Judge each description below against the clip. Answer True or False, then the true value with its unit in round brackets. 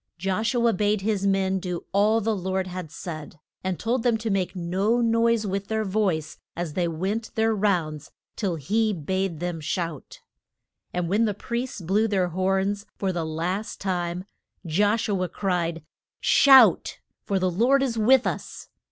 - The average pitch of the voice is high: True (195 Hz)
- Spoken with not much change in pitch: False (3.6 semitones)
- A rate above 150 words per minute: True (170 wpm)